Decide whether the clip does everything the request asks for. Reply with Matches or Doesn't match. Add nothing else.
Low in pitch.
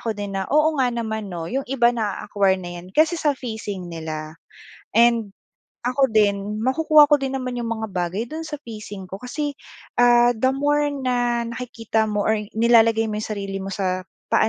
Doesn't match